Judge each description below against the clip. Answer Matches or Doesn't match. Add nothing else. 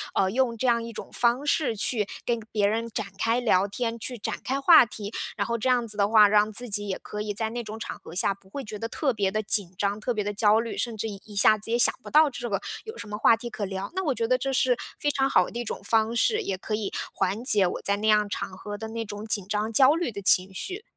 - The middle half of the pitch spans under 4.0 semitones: Matches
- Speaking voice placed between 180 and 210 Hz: Doesn't match